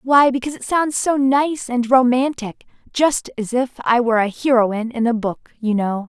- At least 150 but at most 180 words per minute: No, average, 195 wpm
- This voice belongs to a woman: Yes, female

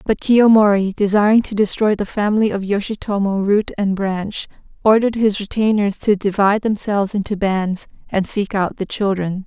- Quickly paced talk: No, average, 160 wpm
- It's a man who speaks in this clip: No, female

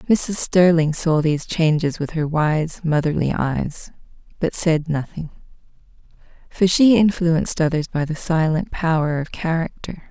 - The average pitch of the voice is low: No, medium, 160 Hz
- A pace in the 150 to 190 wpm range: No, slow, 135 wpm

